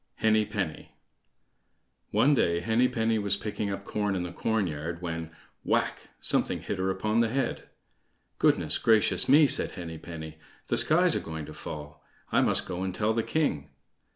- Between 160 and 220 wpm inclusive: Yes, average, 165 wpm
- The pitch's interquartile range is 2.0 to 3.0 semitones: No, average, 4.8 semitones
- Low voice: Yes, low, 100 Hz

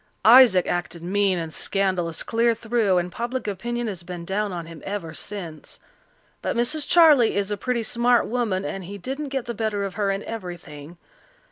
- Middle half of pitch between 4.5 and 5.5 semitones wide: Yes, average, 4.9 semitones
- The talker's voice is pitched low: No, high, 205 Hz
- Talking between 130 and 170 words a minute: No, average, 180 wpm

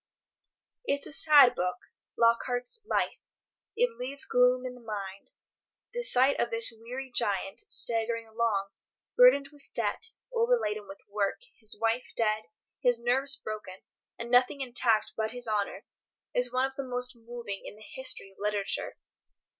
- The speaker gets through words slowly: No, average, 150 wpm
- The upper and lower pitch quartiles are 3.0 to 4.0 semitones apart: Yes, average, 3.4 semitones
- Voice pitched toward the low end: No, high, 240 Hz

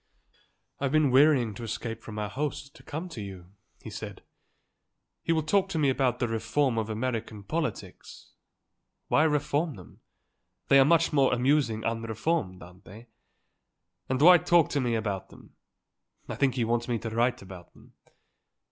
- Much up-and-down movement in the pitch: No, average, 4.8 semitones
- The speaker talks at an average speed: Yes, average, 165 wpm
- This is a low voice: Yes, low, 125 Hz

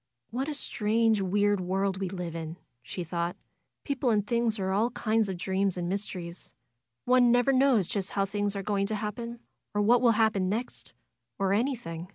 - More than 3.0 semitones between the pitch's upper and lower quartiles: Yes, average, 3.7 semitones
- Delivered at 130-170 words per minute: No, average, 190 wpm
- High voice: Yes, high, 205 Hz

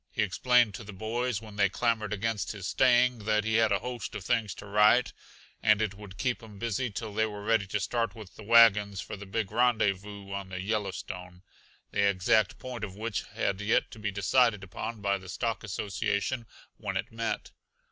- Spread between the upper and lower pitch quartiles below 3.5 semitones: Yes, narrow, 2.6 semitones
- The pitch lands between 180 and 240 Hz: No, low, 105 Hz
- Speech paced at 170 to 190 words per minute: No, average, 200 wpm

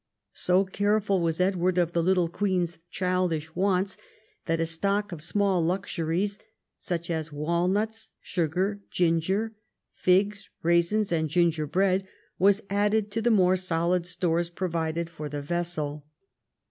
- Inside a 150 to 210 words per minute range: No, slow, 135 wpm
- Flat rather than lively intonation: No, average, 3.0 semitones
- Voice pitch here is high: No, medium, 180 Hz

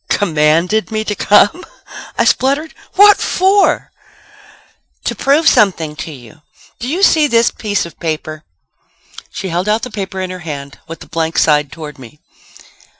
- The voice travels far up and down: Yes, wide, 7.0 semitones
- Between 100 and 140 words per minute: No, average, 155 wpm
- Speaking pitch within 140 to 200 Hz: Yes, high, 190 Hz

